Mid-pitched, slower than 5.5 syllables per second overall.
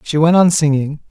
Yes: medium, 155 Hz; 5.3 syllables/s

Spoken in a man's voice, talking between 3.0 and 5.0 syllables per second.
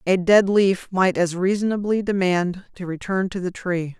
No: female; 4.6 syllables/s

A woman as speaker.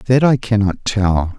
No: male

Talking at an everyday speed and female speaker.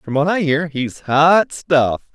No: average, 195 wpm; male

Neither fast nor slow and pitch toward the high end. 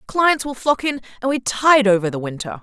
No: fast, 230 wpm; high, 235 Hz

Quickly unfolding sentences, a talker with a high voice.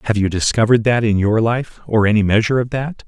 No: fast, 235 wpm; low, 110 Hz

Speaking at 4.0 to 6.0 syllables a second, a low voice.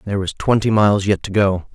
No: 6.3 syllables/s; low, 100 Hz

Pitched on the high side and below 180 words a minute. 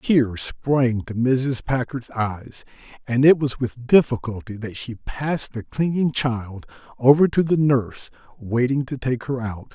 No: low, 125 Hz; average, 160 wpm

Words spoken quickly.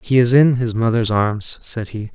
Yes: fast, 225 wpm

